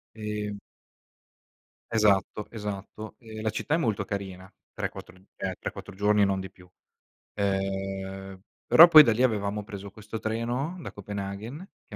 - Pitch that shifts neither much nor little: No, narrow, 2.1 semitones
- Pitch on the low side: Yes, low, 105 Hz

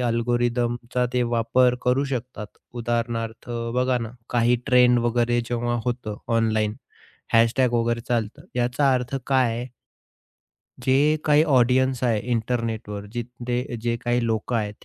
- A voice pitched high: No, low, 120 Hz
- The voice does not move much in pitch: Yes, narrow, 1.3 semitones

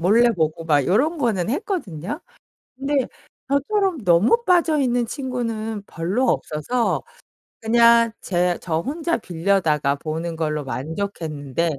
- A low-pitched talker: No, high, 205 Hz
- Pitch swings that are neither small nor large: No, wide, 7.7 semitones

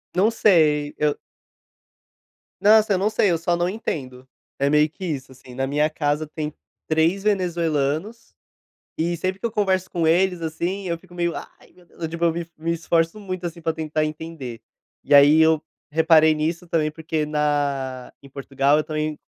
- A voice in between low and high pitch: Yes, medium, 160 Hz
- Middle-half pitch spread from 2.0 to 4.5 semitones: Yes, average, 2.8 semitones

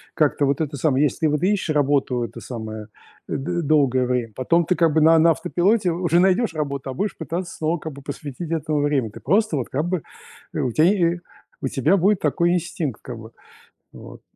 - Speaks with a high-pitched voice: No, medium, 155 Hz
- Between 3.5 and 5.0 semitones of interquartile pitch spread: Yes, average, 4.2 semitones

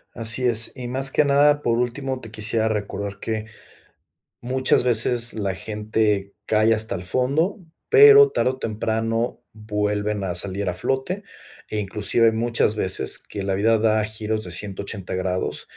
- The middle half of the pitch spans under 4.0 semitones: Yes, average, 3.1 semitones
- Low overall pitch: Yes, low, 110 Hz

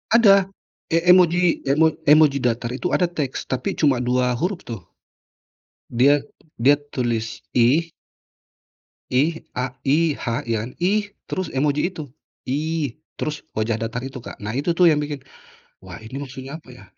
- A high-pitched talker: No, medium, 140 Hz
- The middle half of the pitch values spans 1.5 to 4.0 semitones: No, average, 4.5 semitones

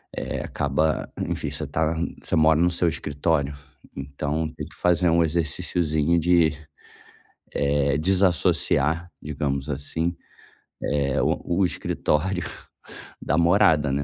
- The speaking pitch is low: Yes, very low, 80 Hz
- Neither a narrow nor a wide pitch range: Yes, average, 3.0 semitones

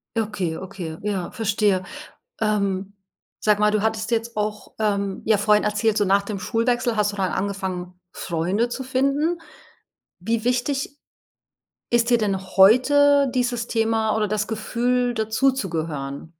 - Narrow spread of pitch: No, average, 3.2 semitones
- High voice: Yes, high, 215 Hz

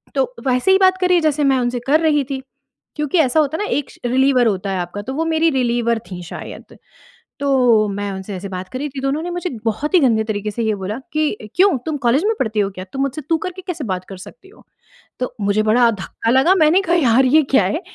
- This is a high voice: Yes, very high, 260 Hz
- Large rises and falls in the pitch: Yes, wide, 6.5 semitones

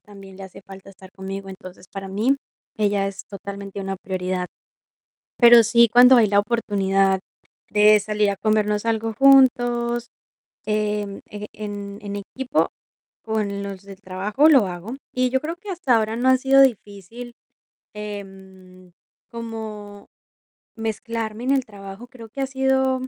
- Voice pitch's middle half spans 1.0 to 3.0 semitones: No, average, 3.4 semitones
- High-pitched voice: Yes, high, 210 Hz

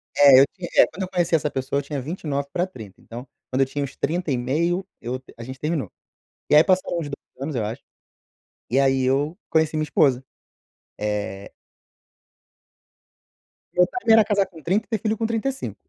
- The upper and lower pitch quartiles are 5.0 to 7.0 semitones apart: Yes, average, 5.3 semitones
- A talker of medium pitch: Yes, medium, 150 Hz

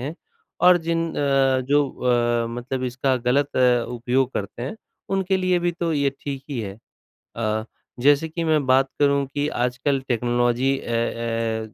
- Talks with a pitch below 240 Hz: Yes, low, 135 Hz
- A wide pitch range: No, average, 3.3 semitones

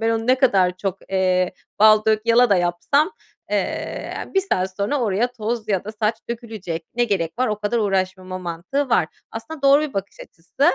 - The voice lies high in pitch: Yes, high, 215 Hz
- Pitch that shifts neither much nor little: Yes, average, 4.3 semitones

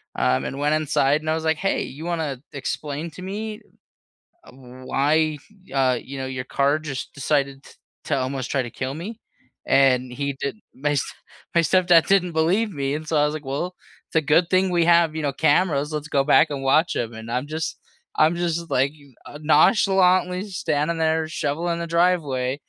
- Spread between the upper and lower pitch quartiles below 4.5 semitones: Yes, average, 3.6 semitones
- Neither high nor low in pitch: Yes, medium, 150 Hz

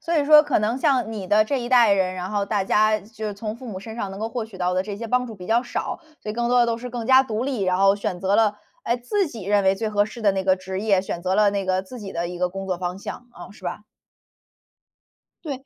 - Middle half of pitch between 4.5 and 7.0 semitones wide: No, average, 3.7 semitones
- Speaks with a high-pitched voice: Yes, high, 210 Hz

